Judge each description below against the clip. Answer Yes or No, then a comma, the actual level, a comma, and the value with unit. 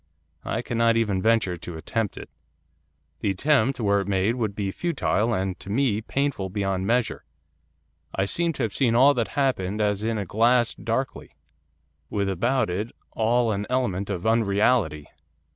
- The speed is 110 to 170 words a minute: Yes, average, 160 wpm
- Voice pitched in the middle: No, low, 110 Hz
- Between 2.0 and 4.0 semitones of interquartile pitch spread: Yes, average, 3.6 semitones